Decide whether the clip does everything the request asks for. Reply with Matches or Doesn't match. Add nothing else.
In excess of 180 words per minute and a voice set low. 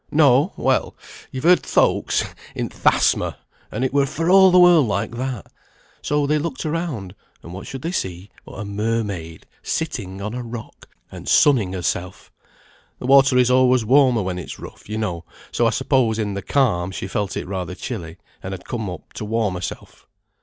Matches